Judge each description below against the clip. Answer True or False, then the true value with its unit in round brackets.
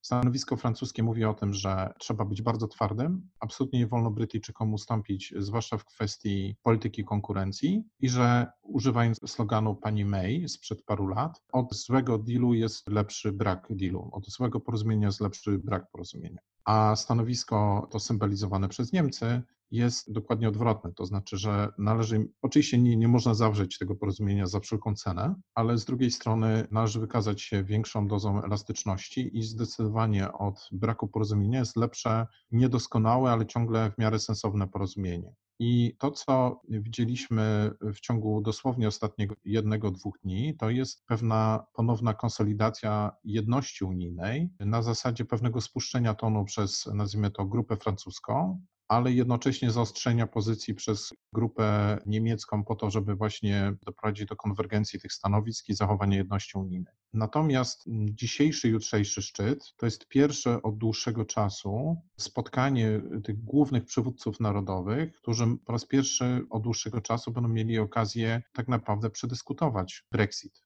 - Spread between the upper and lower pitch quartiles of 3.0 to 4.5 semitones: False (2.5 semitones)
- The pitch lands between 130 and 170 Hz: False (110 Hz)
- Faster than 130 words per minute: True (140 wpm)